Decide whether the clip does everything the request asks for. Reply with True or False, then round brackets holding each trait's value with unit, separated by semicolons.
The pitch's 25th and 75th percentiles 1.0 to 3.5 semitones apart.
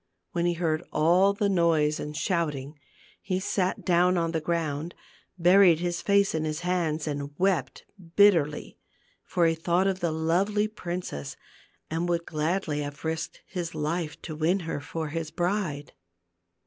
True (2.8 semitones)